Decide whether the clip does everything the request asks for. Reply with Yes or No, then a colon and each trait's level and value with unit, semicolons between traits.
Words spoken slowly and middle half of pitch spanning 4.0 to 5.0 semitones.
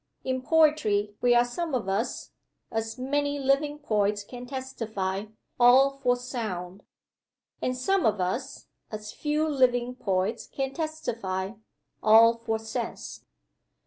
Yes: slow, 125 wpm; average, 4.4 semitones